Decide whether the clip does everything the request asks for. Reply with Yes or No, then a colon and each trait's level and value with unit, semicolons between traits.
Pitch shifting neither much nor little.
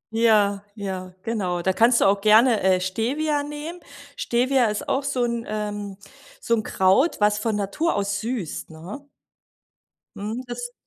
Yes: average, 3.6 semitones